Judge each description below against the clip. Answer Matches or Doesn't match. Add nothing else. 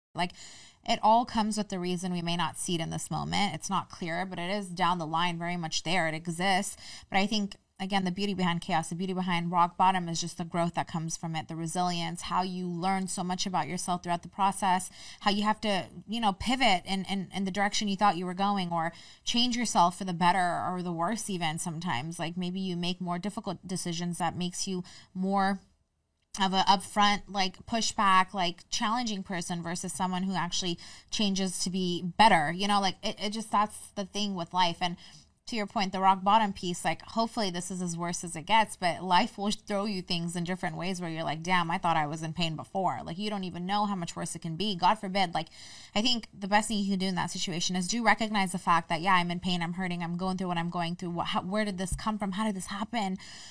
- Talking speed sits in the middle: Doesn't match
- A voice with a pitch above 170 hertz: Matches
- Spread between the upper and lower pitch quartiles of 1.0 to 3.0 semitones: Matches